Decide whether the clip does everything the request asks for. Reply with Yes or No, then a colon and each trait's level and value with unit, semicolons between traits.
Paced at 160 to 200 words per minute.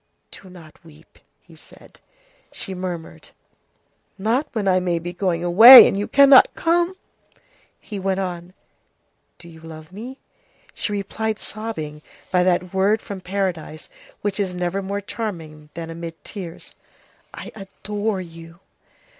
No: average, 140 wpm